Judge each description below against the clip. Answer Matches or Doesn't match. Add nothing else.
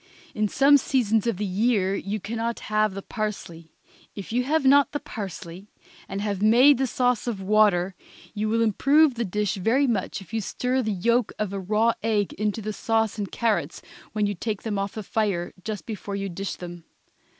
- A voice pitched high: Matches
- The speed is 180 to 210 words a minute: Matches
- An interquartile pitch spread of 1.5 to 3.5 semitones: Matches